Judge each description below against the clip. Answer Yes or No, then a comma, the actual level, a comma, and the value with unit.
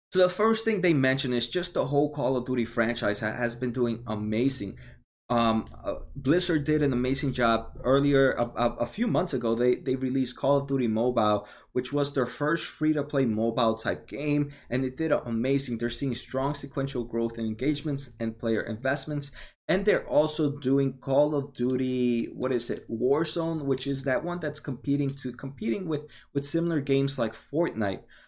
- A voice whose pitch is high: No, low, 130 Hz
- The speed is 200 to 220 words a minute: No, average, 190 wpm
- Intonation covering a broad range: No, average, 3.4 semitones